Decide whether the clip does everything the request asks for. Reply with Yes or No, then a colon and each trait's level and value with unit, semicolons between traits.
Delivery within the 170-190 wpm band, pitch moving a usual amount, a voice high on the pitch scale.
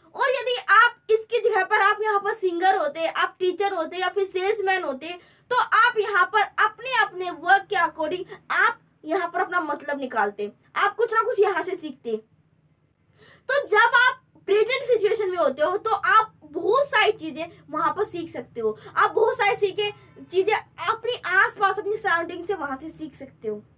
Yes: average, 185 wpm; average, 4.7 semitones; very high, 390 Hz